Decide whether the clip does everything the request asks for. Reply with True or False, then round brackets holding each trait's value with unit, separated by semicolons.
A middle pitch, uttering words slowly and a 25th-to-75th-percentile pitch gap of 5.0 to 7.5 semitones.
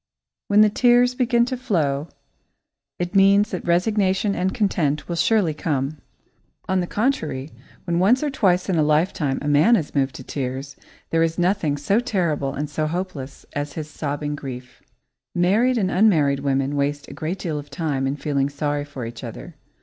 False (160 Hz; 180 wpm; 5.4 semitones)